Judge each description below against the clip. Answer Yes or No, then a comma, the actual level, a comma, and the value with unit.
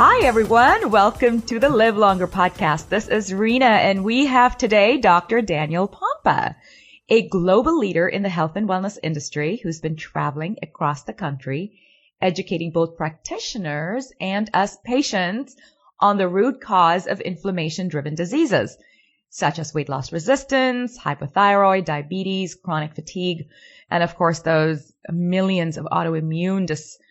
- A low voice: No, medium, 185 Hz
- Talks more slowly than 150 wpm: Yes, average, 140 wpm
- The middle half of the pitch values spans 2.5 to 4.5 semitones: No, average, 5.3 semitones